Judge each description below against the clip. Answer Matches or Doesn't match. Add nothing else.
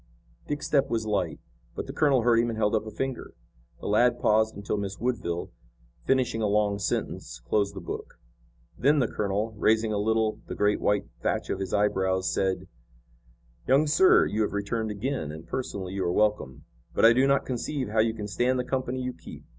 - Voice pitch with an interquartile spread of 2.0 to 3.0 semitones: Doesn't match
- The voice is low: Matches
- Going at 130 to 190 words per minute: Doesn't match